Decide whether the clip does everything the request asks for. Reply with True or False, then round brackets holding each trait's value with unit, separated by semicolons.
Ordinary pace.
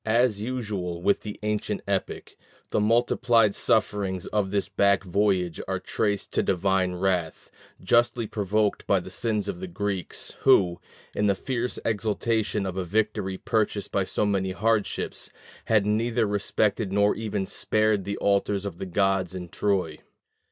True (150 wpm)